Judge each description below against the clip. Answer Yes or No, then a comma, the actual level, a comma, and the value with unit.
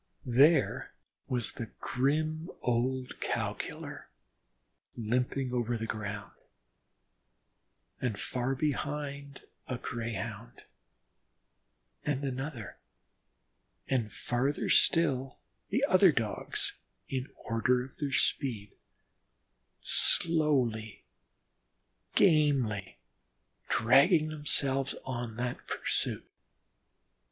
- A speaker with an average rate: No, slow, 80 wpm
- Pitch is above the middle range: No, low, 130 Hz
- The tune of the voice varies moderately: Yes, average, 3.7 semitones